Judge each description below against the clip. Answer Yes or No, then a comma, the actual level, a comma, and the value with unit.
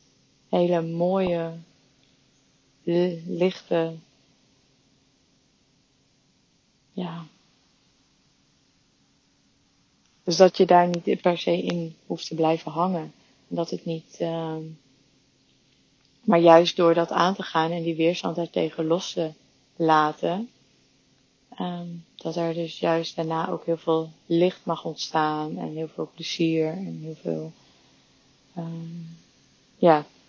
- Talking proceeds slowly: Yes, slow, 115 wpm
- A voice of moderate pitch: Yes, medium, 165 Hz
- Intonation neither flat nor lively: No, narrow, 1.4 semitones